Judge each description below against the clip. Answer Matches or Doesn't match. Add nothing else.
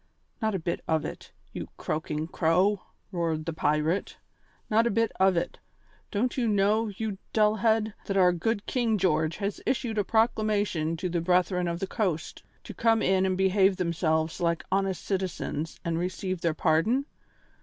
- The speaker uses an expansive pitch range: Doesn't match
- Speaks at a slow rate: Doesn't match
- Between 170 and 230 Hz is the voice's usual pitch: Matches